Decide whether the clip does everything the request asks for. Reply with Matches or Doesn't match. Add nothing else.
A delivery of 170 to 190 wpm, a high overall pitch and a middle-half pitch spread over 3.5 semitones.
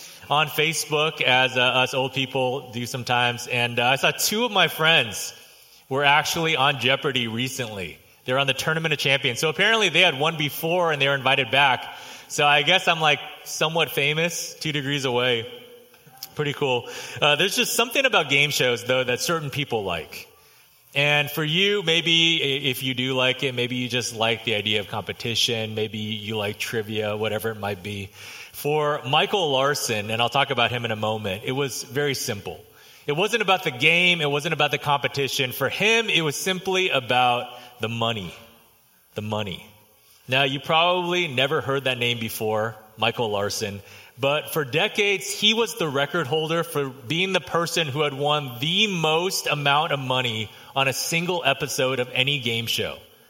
Doesn't match